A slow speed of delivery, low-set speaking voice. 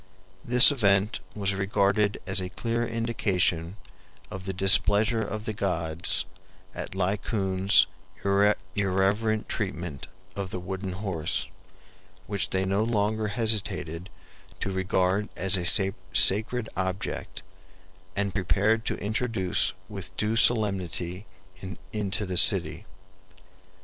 Yes: slow, 110 wpm; low, 100 Hz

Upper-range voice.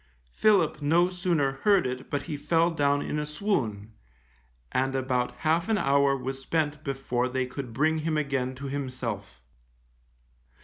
No: medium, 140 Hz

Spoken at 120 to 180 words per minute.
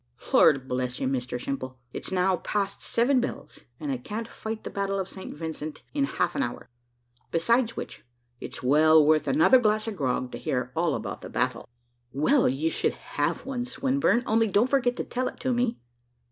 No: average, 190 wpm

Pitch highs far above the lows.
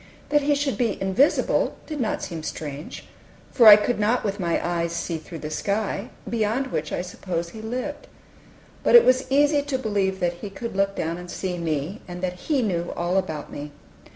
Yes: wide, 6.3 semitones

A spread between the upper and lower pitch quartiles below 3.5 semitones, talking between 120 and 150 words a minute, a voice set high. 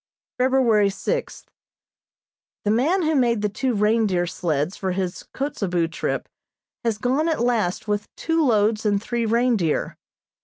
No: average, 4.2 semitones; average, 140 wpm; high, 220 Hz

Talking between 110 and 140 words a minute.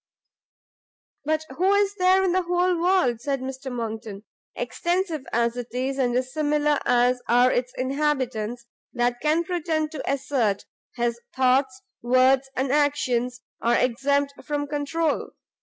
Yes: slow, 135 wpm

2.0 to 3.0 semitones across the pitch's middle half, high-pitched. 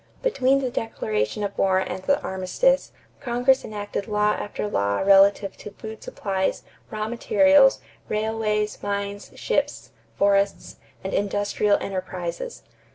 Yes: narrow, 2.4 semitones; high, 205 Hz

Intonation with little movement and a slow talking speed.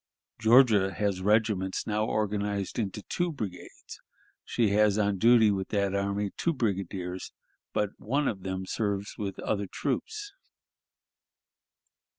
Yes: narrow, 2.1 semitones; slow, 125 wpm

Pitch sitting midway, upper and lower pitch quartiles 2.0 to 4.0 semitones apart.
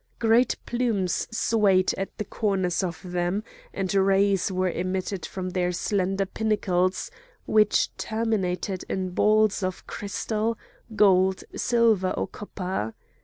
No: high, 195 Hz; narrow, 2.5 semitones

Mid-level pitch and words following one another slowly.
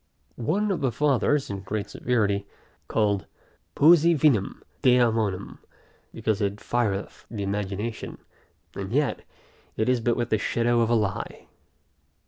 No: low, 115 Hz; slow, 130 wpm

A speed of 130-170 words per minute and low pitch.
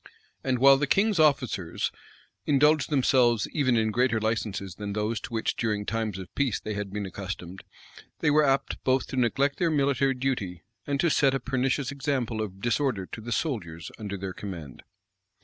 No: average, 180 wpm; low, 120 Hz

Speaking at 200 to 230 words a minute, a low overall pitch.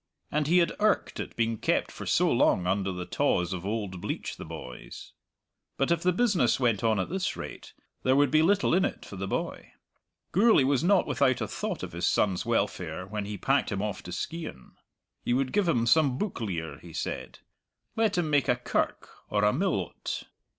Yes: fast, 205 wpm; low, 125 Hz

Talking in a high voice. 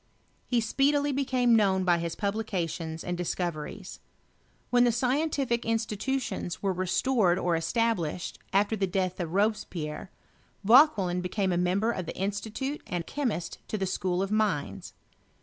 Yes: high, 200 Hz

